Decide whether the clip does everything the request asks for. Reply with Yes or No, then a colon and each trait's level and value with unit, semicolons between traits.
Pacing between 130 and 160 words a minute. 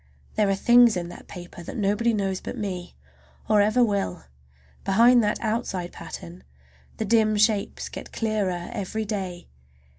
Yes: average, 150 wpm